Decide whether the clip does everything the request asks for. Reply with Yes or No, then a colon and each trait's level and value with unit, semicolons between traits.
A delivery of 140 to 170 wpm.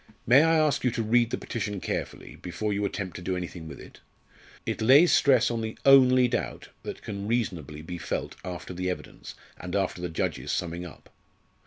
No: average, 195 wpm